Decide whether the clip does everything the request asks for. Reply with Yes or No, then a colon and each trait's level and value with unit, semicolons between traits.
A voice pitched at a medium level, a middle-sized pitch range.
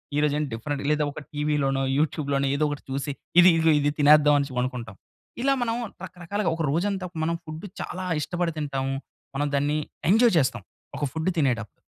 Yes: medium, 150 Hz; average, 3.3 semitones